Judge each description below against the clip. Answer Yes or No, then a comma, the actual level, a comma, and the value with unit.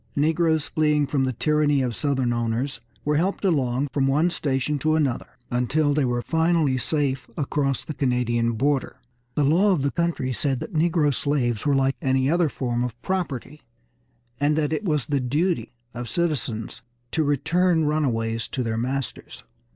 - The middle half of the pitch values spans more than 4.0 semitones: No, average, 3.5 semitones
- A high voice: No, medium, 140 Hz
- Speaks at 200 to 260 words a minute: No, average, 165 wpm